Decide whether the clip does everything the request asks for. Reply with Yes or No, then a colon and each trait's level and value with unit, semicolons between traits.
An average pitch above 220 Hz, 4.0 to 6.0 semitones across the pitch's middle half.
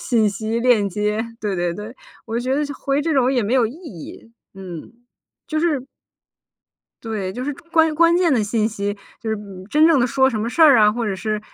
Yes: high, 230 Hz; average, 4.7 semitones